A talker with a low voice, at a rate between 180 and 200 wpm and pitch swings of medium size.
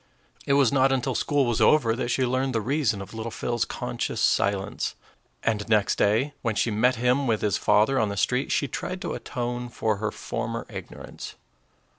Yes: low, 120 Hz; average, 190 wpm; average, 3.3 semitones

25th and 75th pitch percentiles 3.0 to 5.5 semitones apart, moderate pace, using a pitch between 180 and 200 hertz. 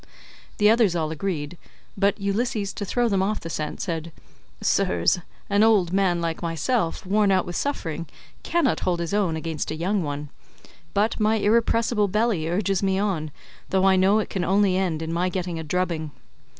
Yes: average, 3.9 semitones; average, 180 wpm; high, 190 Hz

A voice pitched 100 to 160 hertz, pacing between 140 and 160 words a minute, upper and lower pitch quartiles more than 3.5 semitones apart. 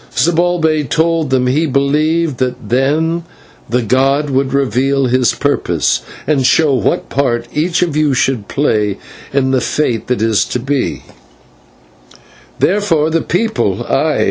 Yes: medium, 140 Hz; average, 145 wpm; average, 4.0 semitones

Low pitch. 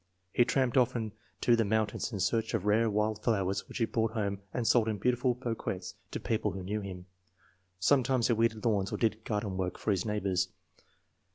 Yes: low, 110 Hz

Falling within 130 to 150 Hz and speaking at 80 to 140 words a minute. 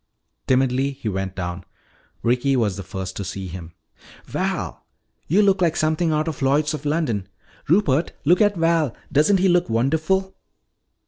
No: medium, 140 Hz; average, 155 wpm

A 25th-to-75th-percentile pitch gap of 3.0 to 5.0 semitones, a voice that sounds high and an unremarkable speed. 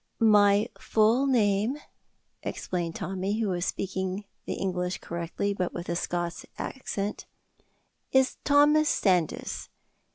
No: average, 3.6 semitones; high, 195 Hz; slow, 110 wpm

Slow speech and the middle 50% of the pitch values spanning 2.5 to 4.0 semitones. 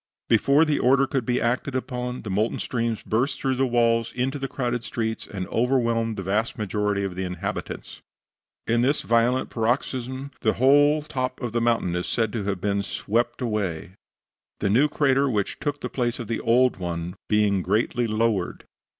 No: average, 180 wpm; average, 3.5 semitones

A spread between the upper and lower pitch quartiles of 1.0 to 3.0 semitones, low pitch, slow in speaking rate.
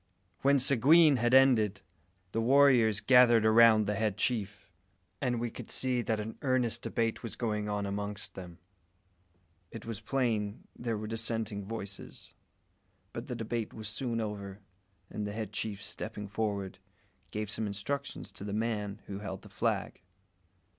No: narrow, 2.5 semitones; low, 110 Hz; average, 155 wpm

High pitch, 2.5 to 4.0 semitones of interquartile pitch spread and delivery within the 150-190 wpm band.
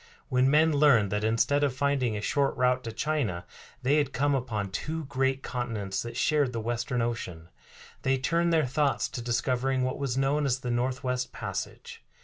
No: low, 130 Hz; average, 3.1 semitones; average, 180 wpm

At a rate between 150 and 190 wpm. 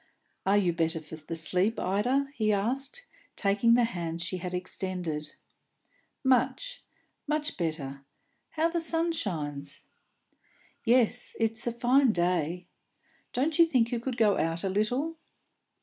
No: slow, 135 wpm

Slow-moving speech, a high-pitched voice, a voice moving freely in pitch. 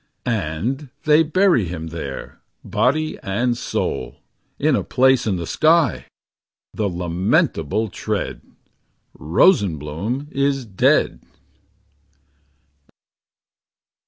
No: slow, 85 wpm; low, 110 Hz; wide, 8.6 semitones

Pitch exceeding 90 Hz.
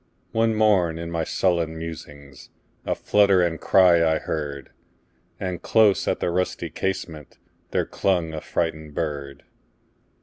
No: very low, 85 Hz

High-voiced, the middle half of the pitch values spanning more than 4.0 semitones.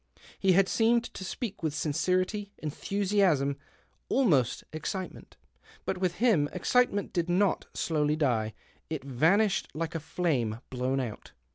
No: medium, 170 Hz; average, 5.3 semitones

